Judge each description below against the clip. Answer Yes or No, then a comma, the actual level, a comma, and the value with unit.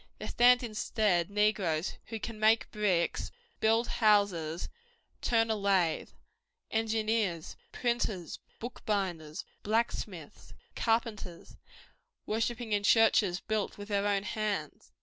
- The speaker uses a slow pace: Yes, slow, 105 wpm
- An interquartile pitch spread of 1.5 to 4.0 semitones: Yes, average, 3.0 semitones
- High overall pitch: Yes, high, 210 Hz